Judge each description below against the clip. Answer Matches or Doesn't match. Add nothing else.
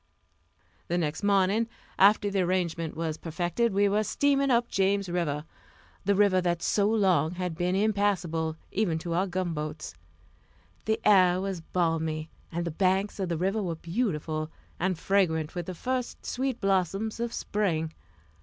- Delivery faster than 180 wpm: Doesn't match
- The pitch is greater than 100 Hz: Matches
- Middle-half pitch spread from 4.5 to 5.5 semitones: Doesn't match